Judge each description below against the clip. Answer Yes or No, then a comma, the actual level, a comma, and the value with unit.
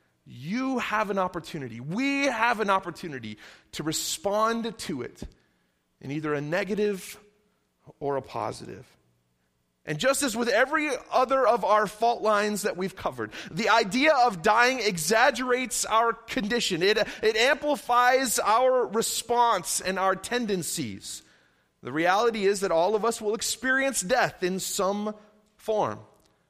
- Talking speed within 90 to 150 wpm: Yes, slow, 135 wpm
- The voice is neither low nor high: No, high, 210 Hz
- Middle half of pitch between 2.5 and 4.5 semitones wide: No, wide, 5.5 semitones